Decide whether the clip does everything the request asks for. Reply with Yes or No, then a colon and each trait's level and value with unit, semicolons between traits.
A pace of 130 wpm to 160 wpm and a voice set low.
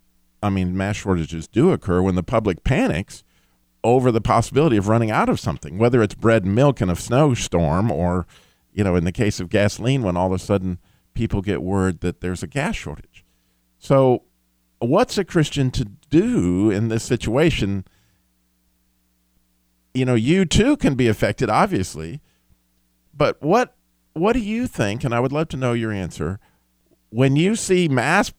No: average, 175 wpm; low, 100 Hz